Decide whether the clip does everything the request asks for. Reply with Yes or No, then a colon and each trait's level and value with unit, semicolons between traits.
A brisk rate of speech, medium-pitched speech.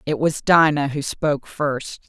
No: average, 175 wpm; medium, 145 Hz